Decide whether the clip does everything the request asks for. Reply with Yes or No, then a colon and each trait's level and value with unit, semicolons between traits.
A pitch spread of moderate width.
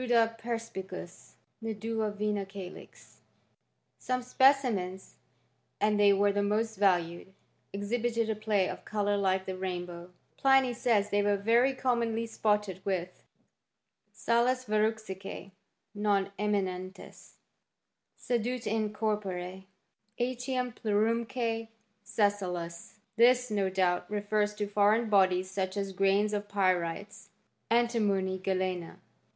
Yes: average, 3.1 semitones